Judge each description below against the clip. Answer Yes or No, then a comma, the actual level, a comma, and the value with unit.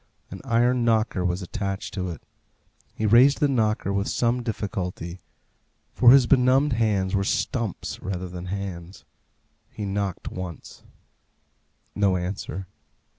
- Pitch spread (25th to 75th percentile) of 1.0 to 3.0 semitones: No, average, 4.2 semitones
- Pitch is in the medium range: No, low, 100 Hz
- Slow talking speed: Yes, slow, 125 wpm